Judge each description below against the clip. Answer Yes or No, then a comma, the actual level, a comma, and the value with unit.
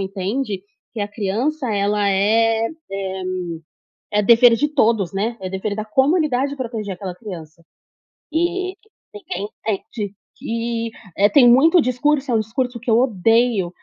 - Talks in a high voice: Yes, high, 225 Hz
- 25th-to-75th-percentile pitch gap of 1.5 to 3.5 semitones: No, average, 4.2 semitones